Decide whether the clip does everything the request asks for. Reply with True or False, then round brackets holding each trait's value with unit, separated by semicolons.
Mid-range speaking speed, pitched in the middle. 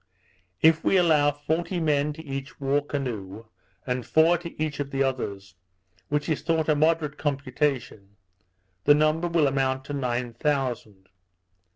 True (150 wpm; 145 Hz)